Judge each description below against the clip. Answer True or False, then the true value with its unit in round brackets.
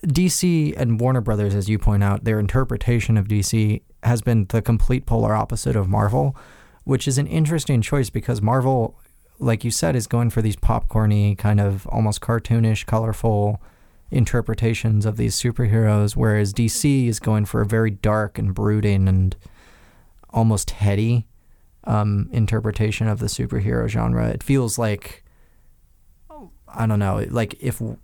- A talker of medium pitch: False (110 Hz)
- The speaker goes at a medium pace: True (150 wpm)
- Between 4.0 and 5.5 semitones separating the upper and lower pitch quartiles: False (2.5 semitones)